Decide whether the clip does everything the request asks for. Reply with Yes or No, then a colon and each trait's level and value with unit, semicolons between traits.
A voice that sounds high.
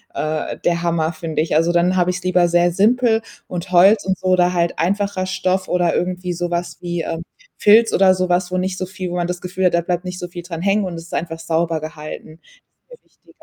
No: medium, 180 Hz